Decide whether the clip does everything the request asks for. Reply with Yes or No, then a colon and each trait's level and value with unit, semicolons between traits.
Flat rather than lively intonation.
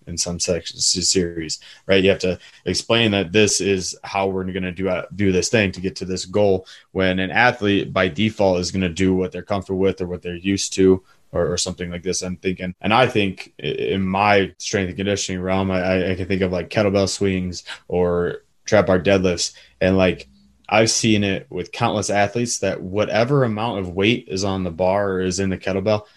Yes: narrow, 1.8 semitones